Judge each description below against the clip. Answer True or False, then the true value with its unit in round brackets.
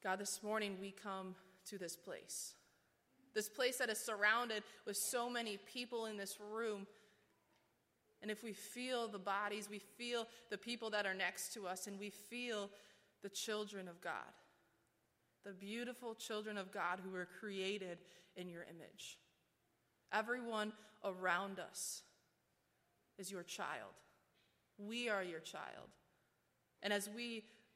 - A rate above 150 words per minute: False (145 wpm)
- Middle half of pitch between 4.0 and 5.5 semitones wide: False (2.5 semitones)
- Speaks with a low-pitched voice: False (205 Hz)